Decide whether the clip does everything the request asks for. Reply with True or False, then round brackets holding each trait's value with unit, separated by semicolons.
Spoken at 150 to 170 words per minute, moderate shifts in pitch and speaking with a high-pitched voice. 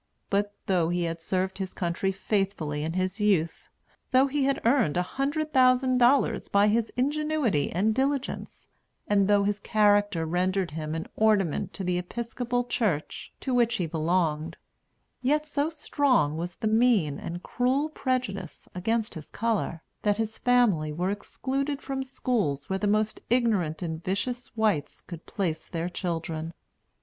False (155 wpm; 6.3 semitones; 205 Hz)